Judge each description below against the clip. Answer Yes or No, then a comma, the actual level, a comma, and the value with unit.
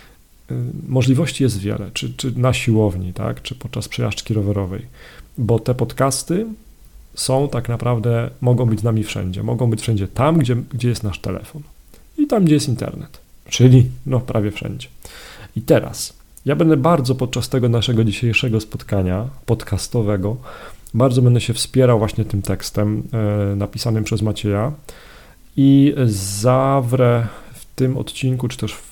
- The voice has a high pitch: No, low, 120 Hz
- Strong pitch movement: No, average, 3.5 semitones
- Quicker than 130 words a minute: Yes, average, 145 wpm